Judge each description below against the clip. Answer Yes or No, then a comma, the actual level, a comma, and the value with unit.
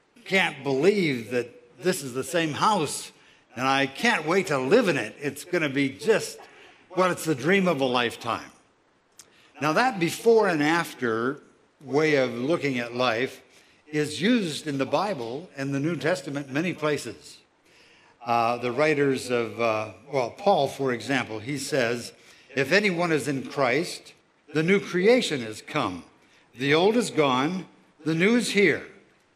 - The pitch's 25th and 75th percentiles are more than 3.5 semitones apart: Yes, average, 5.2 semitones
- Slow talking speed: No, average, 160 wpm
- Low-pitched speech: No, medium, 145 Hz